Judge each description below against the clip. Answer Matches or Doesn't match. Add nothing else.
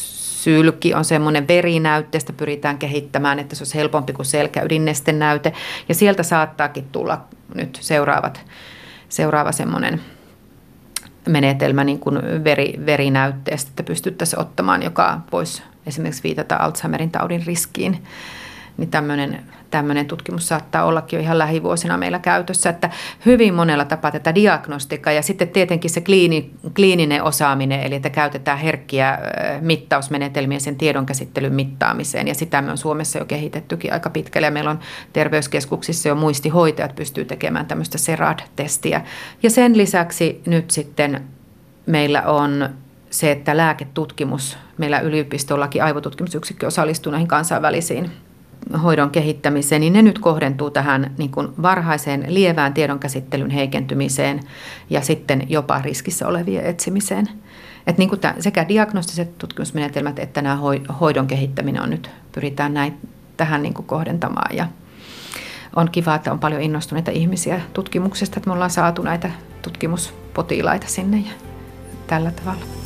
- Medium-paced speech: Matches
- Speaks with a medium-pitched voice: Matches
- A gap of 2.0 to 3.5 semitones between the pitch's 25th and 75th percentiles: Matches